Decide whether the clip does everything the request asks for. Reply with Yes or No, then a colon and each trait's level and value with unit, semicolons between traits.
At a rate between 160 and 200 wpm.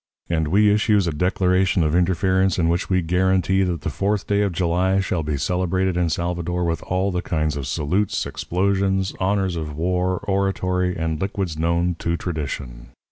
Yes: average, 175 wpm